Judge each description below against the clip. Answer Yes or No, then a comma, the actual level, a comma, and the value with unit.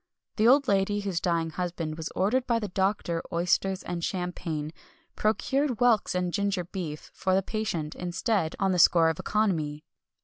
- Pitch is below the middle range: No, medium, 185 Hz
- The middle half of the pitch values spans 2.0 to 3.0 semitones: No, average, 3.8 semitones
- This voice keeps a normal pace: Yes, average, 165 wpm